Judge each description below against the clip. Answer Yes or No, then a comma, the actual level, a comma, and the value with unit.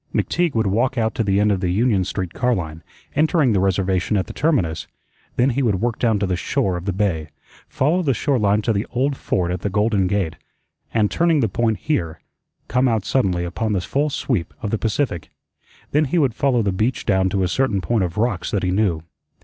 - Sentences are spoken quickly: Yes, fast, 225 wpm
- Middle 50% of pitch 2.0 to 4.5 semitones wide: No, average, 5.0 semitones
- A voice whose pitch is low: Yes, low, 105 Hz